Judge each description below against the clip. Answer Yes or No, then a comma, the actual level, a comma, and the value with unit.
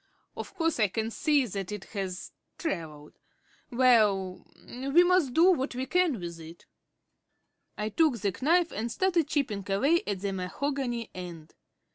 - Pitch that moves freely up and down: Yes, wide, 7.7 semitones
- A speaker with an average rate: Yes, average, 150 wpm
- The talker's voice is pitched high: Yes, high, 235 Hz